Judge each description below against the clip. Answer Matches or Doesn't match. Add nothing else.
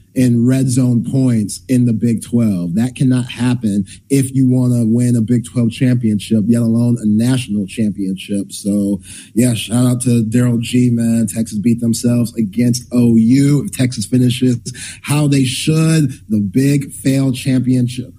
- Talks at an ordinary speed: Matches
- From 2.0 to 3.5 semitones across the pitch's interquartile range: Matches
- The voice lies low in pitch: Matches